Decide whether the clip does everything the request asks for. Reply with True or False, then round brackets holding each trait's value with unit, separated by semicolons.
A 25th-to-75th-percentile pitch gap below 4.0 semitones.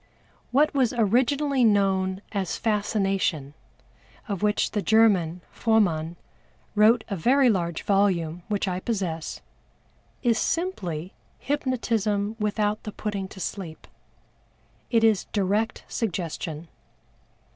True (3.4 semitones)